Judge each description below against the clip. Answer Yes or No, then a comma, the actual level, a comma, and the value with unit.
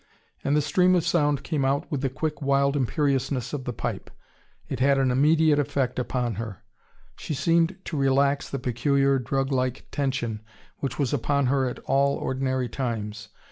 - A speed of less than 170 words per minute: No, average, 175 wpm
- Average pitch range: No, narrow, 2.1 semitones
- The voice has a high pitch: No, low, 135 Hz